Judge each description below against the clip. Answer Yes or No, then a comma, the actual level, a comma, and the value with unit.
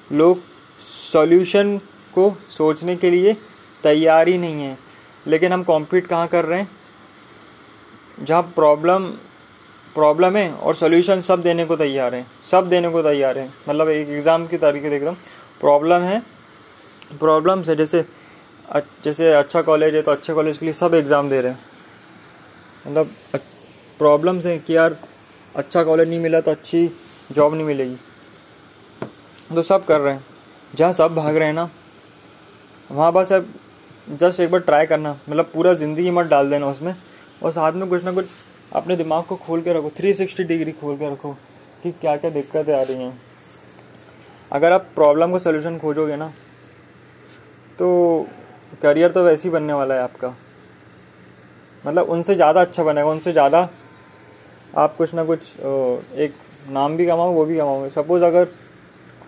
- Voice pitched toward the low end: No, medium, 160 Hz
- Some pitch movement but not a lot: Yes, average, 3.1 semitones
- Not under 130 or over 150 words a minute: No, average, 165 wpm